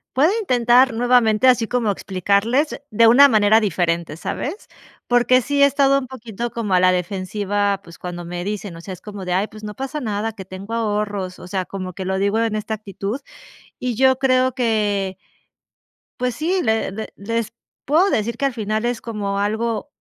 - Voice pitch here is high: Yes, high, 220 Hz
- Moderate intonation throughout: Yes, average, 3.9 semitones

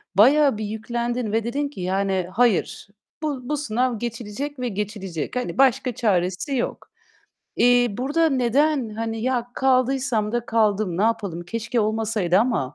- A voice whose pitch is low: No, high, 230 Hz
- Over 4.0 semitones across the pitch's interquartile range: No, average, 3.5 semitones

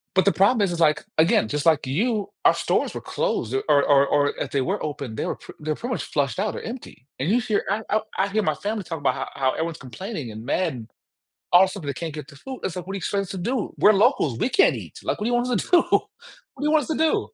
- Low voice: No, medium, 185 Hz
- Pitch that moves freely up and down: Yes, wide, 7.0 semitones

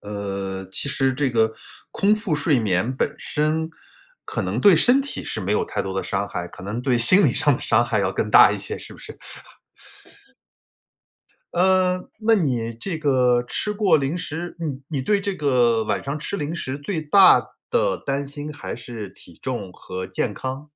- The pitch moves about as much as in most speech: No, wide, 7.0 semitones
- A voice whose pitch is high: No, low, 135 Hz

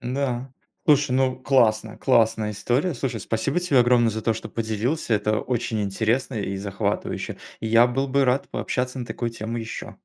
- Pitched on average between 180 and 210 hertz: No, low, 120 Hz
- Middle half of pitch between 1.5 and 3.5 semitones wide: Yes, average, 2.9 semitones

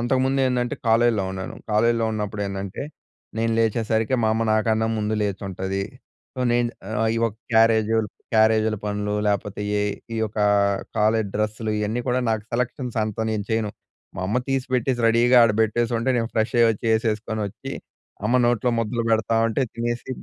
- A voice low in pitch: Yes, low, 110 Hz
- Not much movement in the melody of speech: Yes, narrow, 1.9 semitones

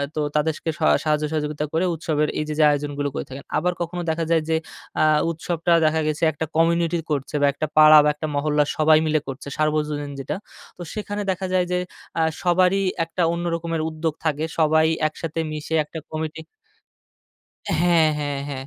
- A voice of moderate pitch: Yes, medium, 155 Hz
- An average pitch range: No, narrow, 1.8 semitones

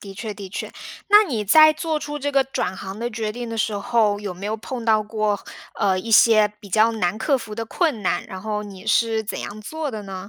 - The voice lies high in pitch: Yes, high, 215 Hz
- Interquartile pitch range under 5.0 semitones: Yes, average, 2.8 semitones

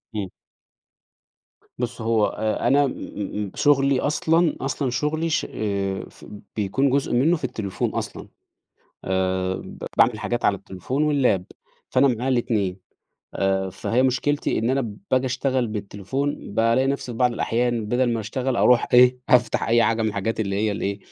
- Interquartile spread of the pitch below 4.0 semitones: No, average, 4.3 semitones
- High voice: No, low, 120 Hz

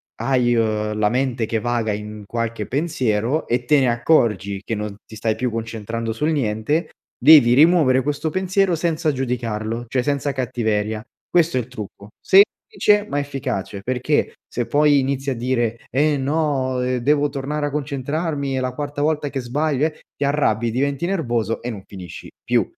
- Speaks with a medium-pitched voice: No, low, 130 Hz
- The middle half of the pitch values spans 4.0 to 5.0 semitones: Yes, average, 4.4 semitones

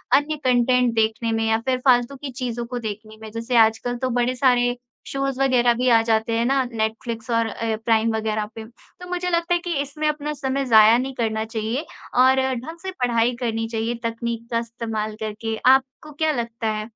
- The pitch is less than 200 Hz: No, high, 235 Hz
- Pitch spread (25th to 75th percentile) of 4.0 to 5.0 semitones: No, average, 2.8 semitones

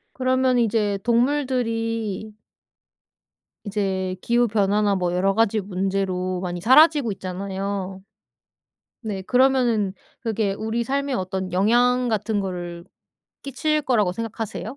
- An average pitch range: Yes, average, 4.0 semitones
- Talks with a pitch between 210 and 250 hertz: Yes, high, 215 Hz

